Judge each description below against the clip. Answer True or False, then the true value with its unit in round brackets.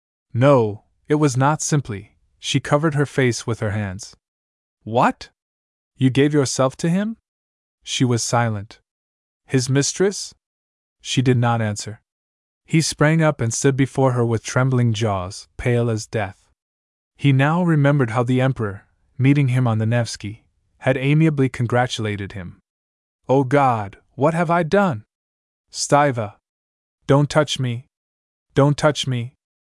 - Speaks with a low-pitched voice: True (120 Hz)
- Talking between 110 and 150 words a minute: True (140 wpm)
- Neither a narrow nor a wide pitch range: False (7.4 semitones)